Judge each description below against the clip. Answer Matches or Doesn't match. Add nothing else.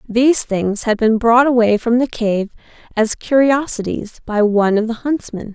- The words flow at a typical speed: Matches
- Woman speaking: Matches